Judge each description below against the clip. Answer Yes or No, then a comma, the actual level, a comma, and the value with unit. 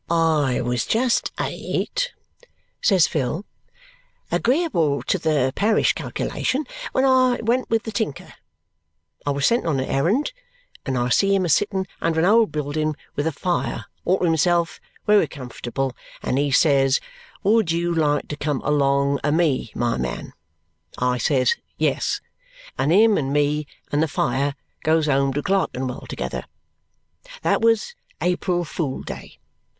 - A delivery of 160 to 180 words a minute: No, average, 150 wpm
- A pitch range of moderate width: No, wide, 6.1 semitones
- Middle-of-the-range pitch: Yes, medium, 155 Hz